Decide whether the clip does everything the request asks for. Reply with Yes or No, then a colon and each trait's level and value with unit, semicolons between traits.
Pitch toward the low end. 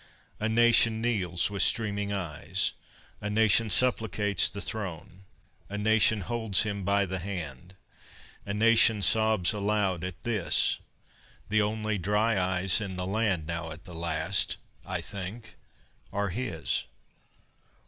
Yes: low, 100 Hz